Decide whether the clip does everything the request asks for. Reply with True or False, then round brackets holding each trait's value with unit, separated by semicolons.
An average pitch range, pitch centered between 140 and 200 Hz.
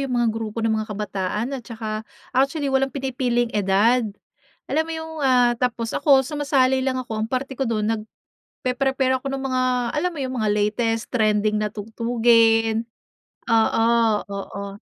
False (3.4 semitones; 240 Hz)